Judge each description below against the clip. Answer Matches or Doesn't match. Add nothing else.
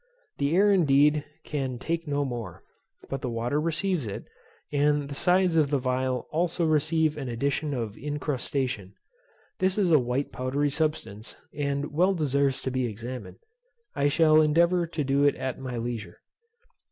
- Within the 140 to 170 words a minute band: Matches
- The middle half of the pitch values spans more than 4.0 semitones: Doesn't match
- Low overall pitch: Doesn't match